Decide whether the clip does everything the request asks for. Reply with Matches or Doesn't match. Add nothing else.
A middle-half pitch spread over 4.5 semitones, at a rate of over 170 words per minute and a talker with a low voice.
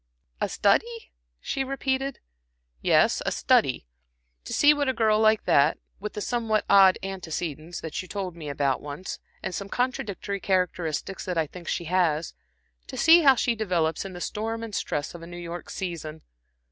Doesn't match